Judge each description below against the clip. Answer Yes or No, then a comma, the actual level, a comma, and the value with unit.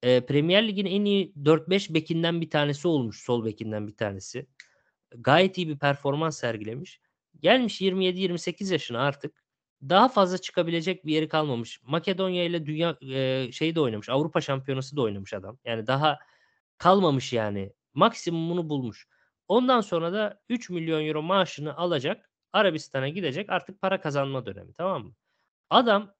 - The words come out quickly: Yes, fast, 145 wpm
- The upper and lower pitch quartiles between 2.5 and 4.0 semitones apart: No, wide, 5.6 semitones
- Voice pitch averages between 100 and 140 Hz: No, medium, 155 Hz